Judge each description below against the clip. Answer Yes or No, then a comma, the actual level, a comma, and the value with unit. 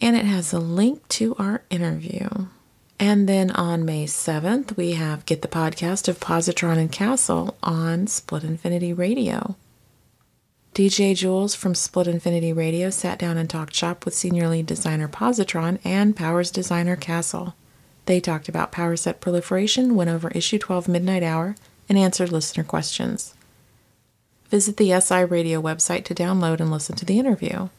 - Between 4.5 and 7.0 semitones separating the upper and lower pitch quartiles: No, average, 2.9 semitones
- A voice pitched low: No, medium, 175 Hz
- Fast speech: No, average, 160 wpm